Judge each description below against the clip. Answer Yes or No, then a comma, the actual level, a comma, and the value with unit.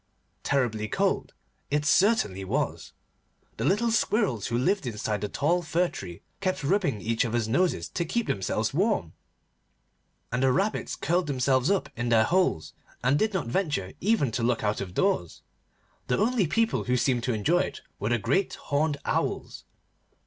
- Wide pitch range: Yes, wide, 8.6 semitones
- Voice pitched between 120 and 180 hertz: Yes, low, 135 Hz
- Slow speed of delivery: No, average, 165 wpm